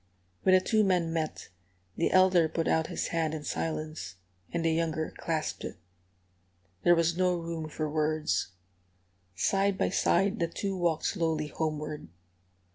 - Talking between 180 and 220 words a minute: No, average, 150 wpm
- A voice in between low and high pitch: Yes, medium, 165 Hz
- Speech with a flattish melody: Yes, narrow, 2.3 semitones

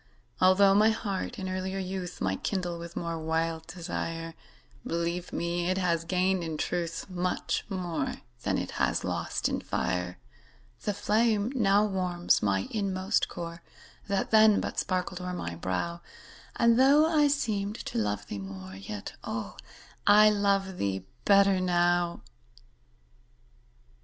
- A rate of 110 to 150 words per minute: Yes, average, 140 wpm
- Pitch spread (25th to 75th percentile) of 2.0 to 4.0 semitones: Yes, average, 3.2 semitones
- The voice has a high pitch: No, medium, 180 Hz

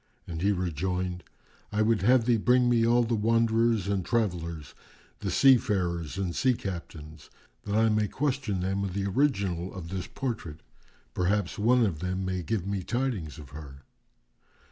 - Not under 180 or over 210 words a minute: No, average, 165 wpm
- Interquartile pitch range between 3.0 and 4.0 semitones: No, average, 4.6 semitones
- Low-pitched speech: Yes, low, 100 Hz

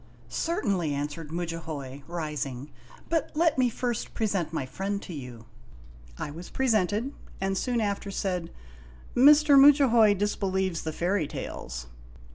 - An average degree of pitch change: No, wide, 7.1 semitones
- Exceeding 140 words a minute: No, slow, 135 wpm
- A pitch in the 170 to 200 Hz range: Yes, high, 190 Hz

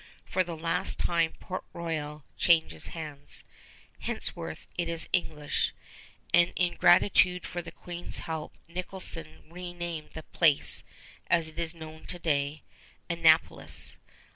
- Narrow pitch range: Yes, narrow, 1.8 semitones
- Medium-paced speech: No, slow, 125 wpm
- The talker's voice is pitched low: No, medium, 165 Hz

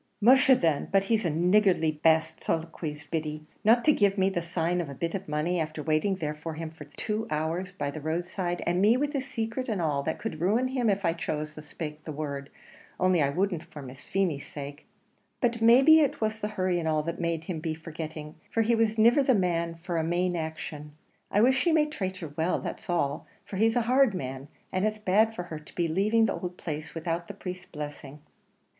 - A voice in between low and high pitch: Yes, medium, 175 Hz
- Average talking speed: No, fast, 225 wpm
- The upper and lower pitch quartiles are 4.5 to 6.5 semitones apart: Yes, wide, 5.4 semitones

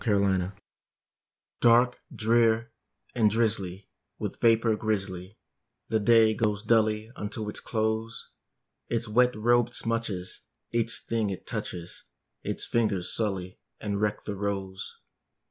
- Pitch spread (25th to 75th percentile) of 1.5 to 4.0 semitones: Yes, narrow, 2.4 semitones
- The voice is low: Yes, low, 110 Hz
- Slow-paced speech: Yes, slow, 125 wpm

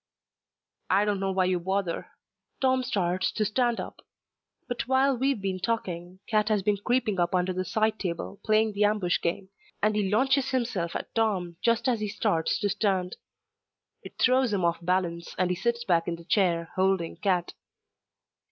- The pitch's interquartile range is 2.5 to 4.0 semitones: Yes, average, 3.6 semitones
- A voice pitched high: Yes, high, 195 Hz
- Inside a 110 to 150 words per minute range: No, average, 180 wpm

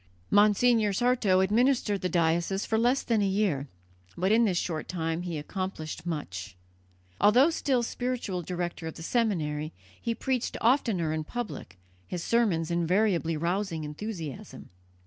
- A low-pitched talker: No, high, 190 Hz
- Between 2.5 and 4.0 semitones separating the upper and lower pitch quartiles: No, wide, 5.4 semitones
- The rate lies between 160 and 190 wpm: No, average, 140 wpm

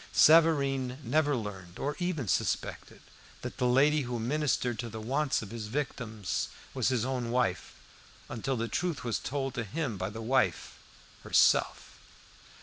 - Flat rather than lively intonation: No, average, 4.1 semitones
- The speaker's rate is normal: Yes, average, 150 wpm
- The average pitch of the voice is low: Yes, low, 125 Hz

